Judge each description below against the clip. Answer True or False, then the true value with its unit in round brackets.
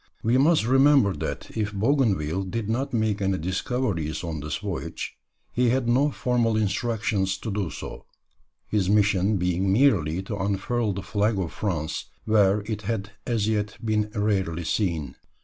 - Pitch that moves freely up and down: False (3.4 semitones)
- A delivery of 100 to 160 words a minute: True (155 wpm)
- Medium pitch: False (105 Hz)